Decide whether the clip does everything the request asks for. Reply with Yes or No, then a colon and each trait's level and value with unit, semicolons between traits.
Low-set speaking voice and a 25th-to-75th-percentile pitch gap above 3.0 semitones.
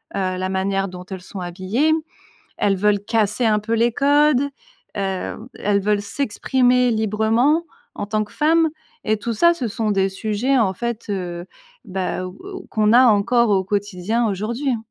No: high, 215 Hz; average, 3.7 semitones